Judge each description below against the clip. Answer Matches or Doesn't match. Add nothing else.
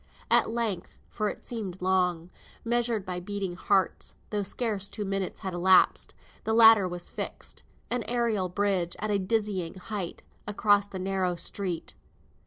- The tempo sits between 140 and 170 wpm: Matches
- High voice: Matches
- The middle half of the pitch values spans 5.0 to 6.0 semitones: Doesn't match